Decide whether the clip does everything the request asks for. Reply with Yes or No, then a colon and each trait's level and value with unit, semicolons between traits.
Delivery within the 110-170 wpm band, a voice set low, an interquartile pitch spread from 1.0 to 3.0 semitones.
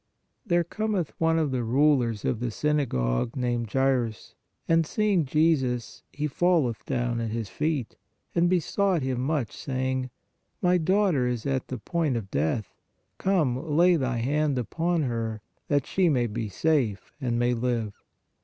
No: average, 155 wpm; low, 130 Hz; average, 5.3 semitones